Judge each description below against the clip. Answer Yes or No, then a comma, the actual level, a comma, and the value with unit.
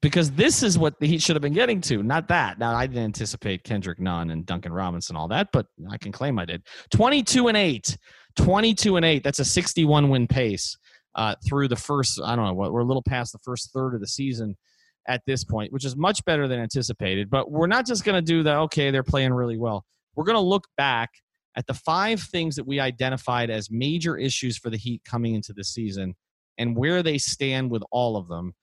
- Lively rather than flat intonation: Yes, wide, 5.8 semitones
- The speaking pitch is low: Yes, low, 130 Hz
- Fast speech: Yes, fast, 235 wpm